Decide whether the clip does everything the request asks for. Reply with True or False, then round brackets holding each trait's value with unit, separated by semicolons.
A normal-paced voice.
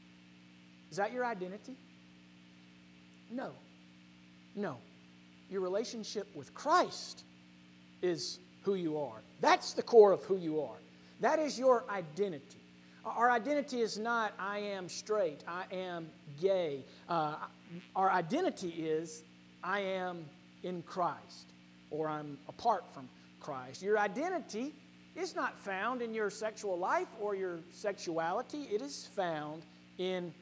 False (130 wpm)